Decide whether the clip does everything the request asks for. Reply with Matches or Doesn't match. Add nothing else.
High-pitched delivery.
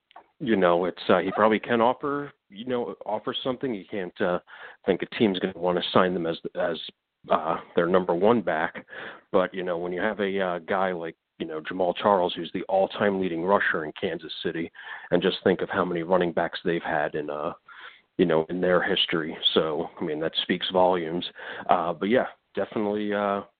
Doesn't match